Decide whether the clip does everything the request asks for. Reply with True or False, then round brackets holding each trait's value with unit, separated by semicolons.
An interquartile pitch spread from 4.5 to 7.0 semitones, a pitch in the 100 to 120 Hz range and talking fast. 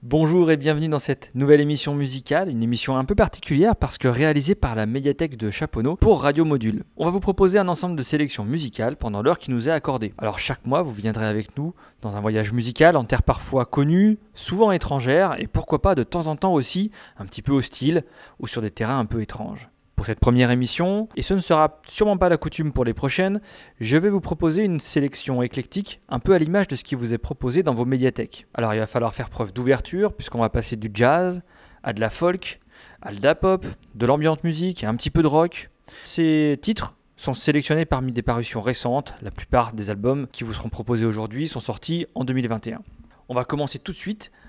False (5.6 semitones; 140 Hz; 225 wpm)